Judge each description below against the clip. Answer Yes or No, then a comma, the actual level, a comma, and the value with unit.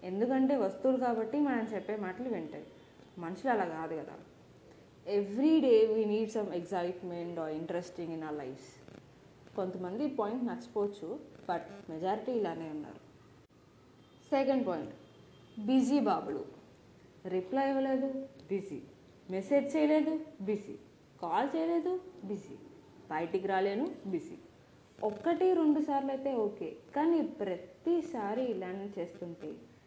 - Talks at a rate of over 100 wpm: Yes, average, 110 wpm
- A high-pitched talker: Yes, high, 210 Hz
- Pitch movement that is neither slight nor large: No, wide, 7.1 semitones